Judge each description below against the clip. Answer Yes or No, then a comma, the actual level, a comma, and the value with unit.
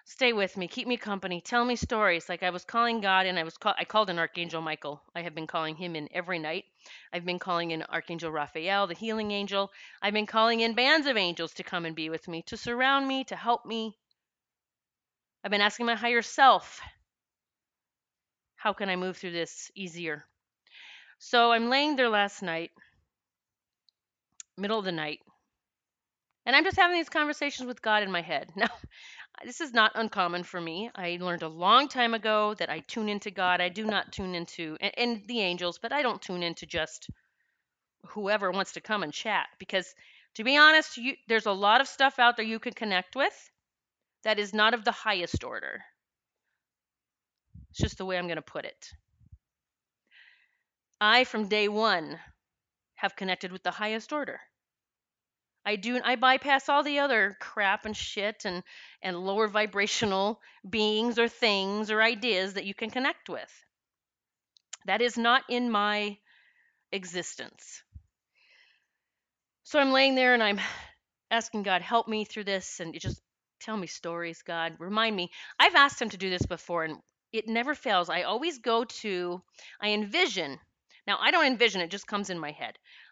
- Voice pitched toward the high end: Yes, high, 210 Hz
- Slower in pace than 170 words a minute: No, average, 180 wpm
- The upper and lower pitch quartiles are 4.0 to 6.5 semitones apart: Yes, average, 4.6 semitones